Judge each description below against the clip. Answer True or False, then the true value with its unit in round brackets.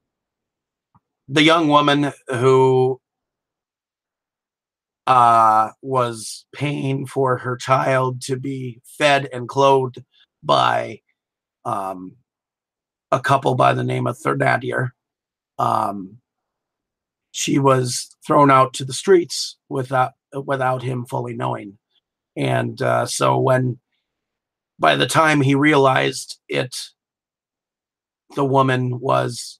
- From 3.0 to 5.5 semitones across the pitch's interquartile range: False (2.5 semitones)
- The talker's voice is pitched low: True (130 Hz)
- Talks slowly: True (100 wpm)